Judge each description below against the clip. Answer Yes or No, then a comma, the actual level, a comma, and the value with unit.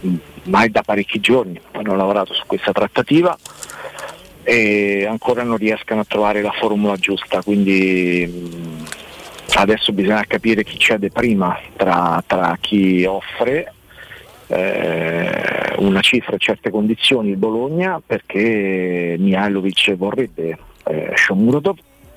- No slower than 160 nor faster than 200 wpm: No, slow, 115 wpm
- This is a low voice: Yes, low, 100 Hz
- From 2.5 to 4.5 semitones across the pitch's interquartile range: Yes, average, 2.8 semitones